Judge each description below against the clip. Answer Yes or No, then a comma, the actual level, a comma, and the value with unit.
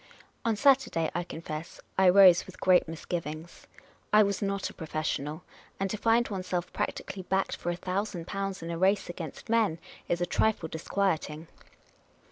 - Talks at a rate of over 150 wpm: Yes, average, 165 wpm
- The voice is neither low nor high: Yes, medium, 180 Hz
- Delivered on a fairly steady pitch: No, average, 3.2 semitones